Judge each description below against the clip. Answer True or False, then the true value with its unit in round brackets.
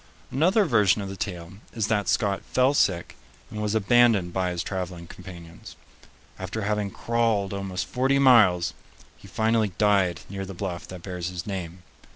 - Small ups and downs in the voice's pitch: False (3.7 semitones)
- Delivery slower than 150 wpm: False (165 wpm)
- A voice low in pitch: True (100 Hz)